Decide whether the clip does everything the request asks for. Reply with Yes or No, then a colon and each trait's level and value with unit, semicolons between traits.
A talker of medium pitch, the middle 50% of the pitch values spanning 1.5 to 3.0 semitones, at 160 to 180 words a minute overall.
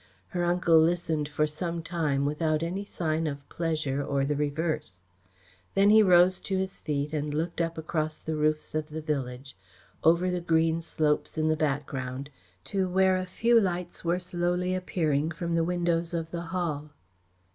Yes: medium, 165 Hz; narrow, 2.6 semitones; average, 170 wpm